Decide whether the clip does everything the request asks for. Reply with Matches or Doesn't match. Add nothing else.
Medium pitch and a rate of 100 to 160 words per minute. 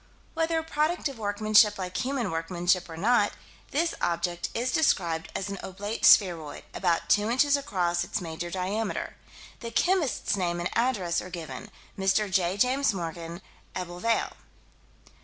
Doesn't match